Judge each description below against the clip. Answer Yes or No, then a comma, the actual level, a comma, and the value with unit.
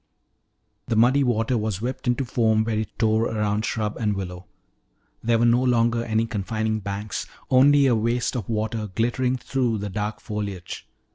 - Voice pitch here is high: No, low, 110 Hz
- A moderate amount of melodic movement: No, narrow, 2.2 semitones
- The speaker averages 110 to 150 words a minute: No, average, 165 wpm